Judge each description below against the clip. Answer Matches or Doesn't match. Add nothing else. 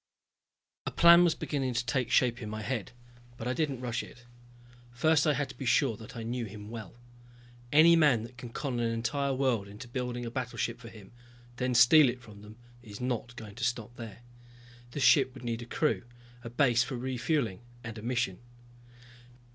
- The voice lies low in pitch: Matches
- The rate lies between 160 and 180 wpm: Doesn't match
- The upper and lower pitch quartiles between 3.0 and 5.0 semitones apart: Doesn't match